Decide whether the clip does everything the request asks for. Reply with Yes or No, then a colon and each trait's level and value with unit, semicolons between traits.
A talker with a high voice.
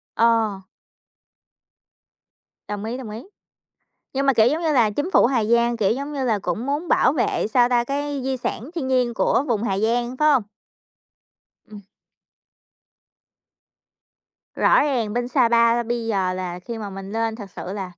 Yes: high, 235 Hz